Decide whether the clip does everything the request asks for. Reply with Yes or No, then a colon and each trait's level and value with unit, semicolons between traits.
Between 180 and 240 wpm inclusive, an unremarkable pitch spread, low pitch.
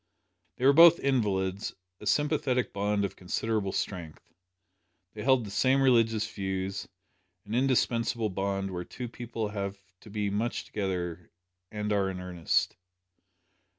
No: slow, 135 wpm; average, 3.8 semitones; low, 105 Hz